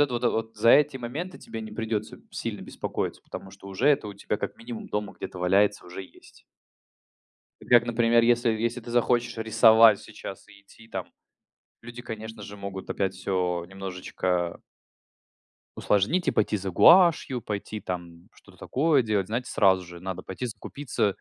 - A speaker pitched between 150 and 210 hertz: No, low, 110 Hz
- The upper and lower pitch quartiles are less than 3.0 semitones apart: No, average, 3.6 semitones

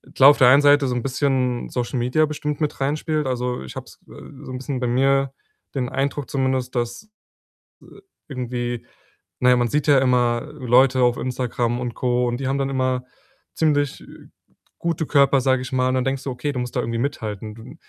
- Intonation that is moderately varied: No, narrow, 2.0 semitones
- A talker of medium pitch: No, low, 130 Hz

